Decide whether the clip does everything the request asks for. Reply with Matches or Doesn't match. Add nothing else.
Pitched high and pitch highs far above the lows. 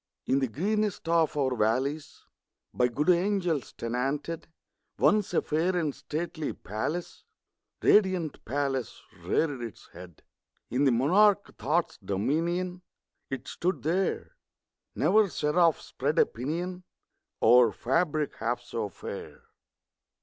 Doesn't match